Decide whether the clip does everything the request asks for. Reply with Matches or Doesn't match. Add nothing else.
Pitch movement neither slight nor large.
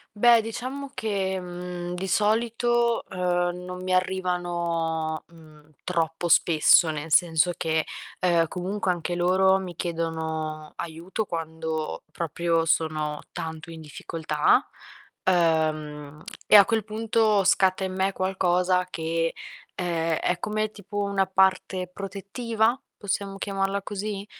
Matches